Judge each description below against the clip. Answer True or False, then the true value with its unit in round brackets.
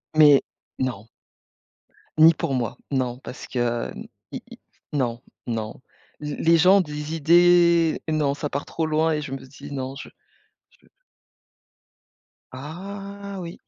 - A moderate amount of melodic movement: True (4.4 semitones)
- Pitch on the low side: False (150 Hz)